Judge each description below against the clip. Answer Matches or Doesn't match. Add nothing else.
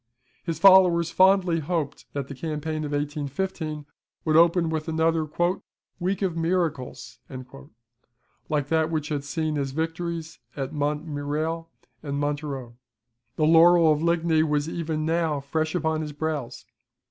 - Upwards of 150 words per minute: Doesn't match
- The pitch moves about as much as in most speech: Doesn't match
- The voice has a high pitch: Doesn't match